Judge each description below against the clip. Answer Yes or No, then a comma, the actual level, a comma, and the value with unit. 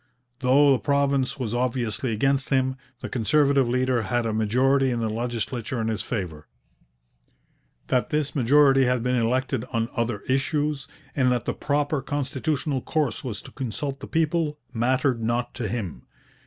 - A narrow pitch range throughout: No, average, 3.0 semitones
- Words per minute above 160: No, average, 155 wpm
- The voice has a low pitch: Yes, low, 130 Hz